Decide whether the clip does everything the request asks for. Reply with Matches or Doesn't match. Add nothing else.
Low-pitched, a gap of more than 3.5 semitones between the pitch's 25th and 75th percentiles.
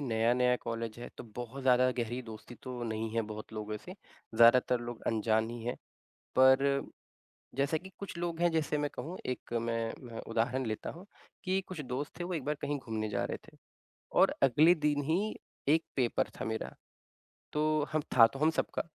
Matches